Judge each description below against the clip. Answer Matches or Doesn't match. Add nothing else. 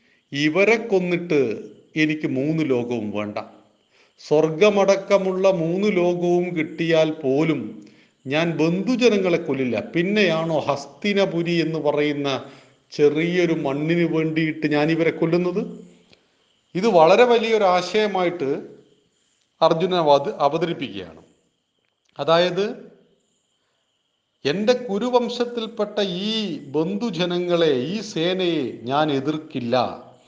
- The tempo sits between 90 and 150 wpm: Doesn't match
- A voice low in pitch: Doesn't match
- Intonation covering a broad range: Doesn't match